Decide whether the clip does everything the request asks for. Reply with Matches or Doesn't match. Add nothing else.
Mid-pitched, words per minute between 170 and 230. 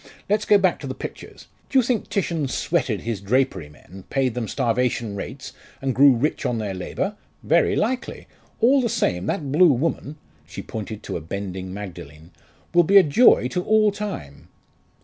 Doesn't match